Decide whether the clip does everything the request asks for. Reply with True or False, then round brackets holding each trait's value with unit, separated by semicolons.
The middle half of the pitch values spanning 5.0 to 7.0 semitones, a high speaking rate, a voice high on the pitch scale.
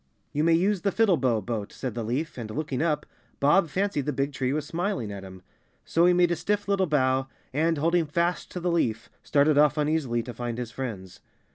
False (5.5 semitones; 215 wpm; 150 Hz)